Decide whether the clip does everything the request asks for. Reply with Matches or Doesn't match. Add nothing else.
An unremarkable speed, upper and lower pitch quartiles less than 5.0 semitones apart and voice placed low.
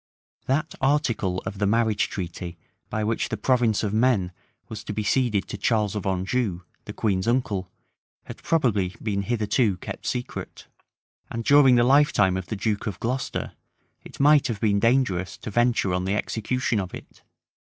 Matches